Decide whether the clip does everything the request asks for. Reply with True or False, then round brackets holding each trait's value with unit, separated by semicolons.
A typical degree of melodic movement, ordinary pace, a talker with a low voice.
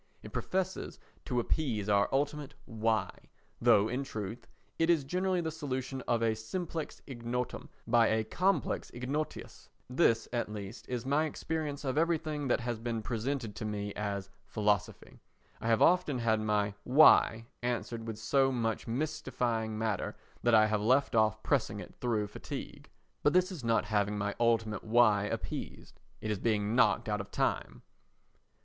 True (4.5 semitones; 160 wpm; 115 Hz)